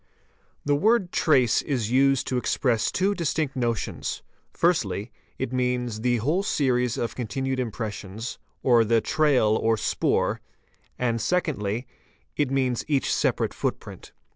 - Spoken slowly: Yes, slow, 120 wpm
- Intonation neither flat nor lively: Yes, average, 3.7 semitones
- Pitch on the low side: Yes, low, 125 Hz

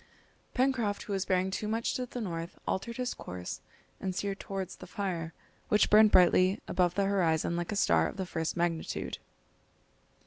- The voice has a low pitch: No, high, 190 Hz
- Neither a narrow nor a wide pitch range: Yes, average, 3.3 semitones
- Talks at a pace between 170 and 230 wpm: Yes, average, 175 wpm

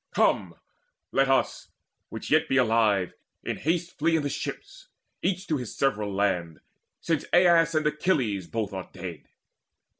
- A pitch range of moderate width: No, wide, 8.3 semitones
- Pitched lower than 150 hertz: Yes, low, 135 Hz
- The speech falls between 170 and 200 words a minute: No, average, 150 wpm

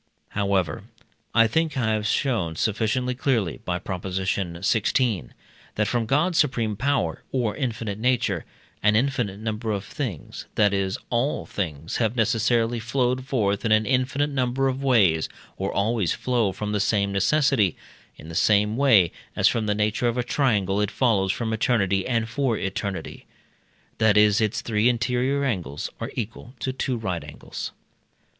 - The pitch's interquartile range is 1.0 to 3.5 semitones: No, average, 4.1 semitones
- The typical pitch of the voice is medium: No, low, 110 Hz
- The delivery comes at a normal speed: Yes, average, 155 wpm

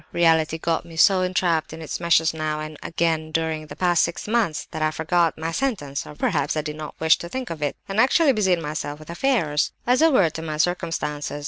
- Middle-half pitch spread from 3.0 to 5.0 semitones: No, narrow, 2.5 semitones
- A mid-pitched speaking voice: Yes, medium, 165 Hz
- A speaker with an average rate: No, fast, 225 wpm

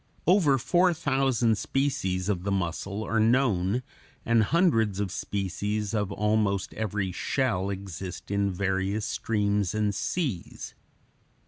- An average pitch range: Yes, average, 3.3 semitones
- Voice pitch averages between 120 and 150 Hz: No, low, 105 Hz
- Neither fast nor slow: No, slow, 120 wpm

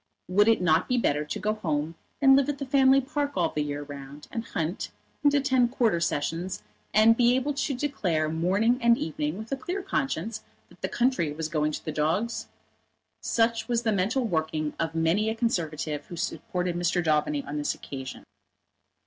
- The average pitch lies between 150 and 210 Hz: Yes, medium, 185 Hz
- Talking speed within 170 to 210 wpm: Yes, average, 190 wpm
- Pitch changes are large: Yes, wide, 7.7 semitones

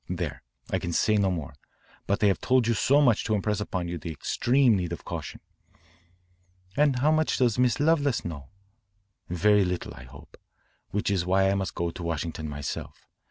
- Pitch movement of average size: No, wide, 6.0 semitones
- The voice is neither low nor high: No, very low, 95 Hz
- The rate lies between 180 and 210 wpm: Yes, average, 190 wpm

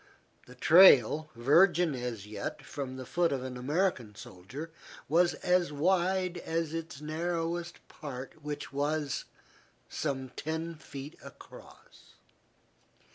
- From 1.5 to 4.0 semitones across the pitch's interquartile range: No, average, 4.6 semitones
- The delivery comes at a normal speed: No, slow, 115 wpm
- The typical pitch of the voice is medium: Yes, medium, 150 Hz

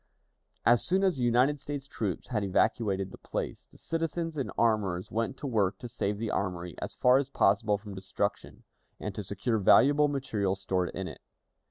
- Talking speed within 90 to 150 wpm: No, average, 185 wpm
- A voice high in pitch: No, low, 110 Hz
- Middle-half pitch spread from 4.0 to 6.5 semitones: Yes, wide, 5.5 semitones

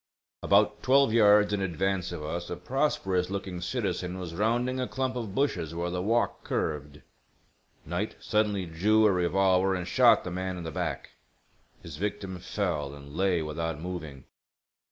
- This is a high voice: No, very low, 95 Hz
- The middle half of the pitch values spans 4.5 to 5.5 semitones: No, average, 3.6 semitones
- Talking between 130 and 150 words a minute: No, average, 160 wpm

